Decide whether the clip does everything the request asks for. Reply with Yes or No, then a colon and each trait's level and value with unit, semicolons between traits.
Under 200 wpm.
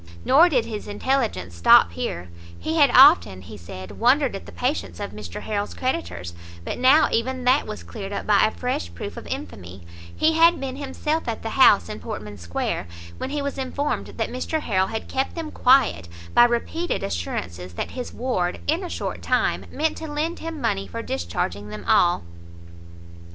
Yes: average, 180 wpm